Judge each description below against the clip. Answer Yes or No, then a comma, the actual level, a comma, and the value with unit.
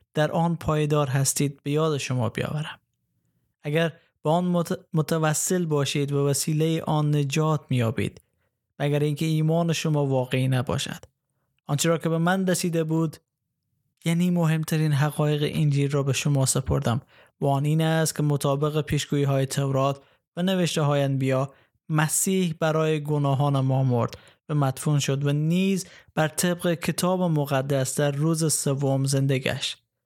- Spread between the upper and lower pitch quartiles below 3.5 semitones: Yes, average, 2.8 semitones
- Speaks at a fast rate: No, average, 140 wpm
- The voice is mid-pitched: Yes, medium, 150 Hz